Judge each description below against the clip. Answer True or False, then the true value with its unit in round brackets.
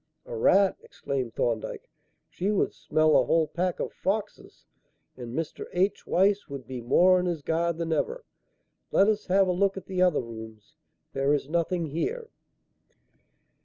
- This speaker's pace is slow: False (165 wpm)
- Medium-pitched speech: True (170 Hz)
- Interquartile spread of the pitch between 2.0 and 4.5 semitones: False (5.5 semitones)